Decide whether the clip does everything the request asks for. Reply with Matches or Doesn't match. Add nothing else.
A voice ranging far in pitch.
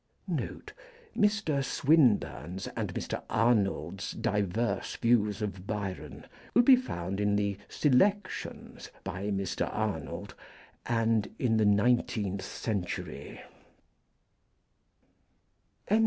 Doesn't match